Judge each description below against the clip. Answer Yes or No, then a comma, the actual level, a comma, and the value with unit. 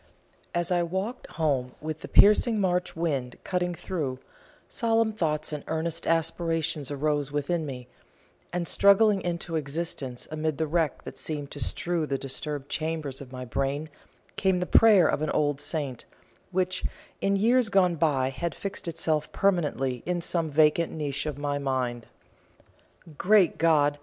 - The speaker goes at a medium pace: Yes, average, 155 wpm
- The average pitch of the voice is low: No, medium, 160 Hz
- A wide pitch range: No, average, 3.7 semitones